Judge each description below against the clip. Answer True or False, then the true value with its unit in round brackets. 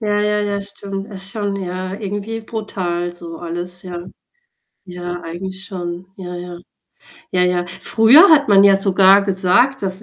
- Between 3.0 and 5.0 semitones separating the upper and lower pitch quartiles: False (2.5 semitones)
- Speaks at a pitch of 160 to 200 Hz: True (190 Hz)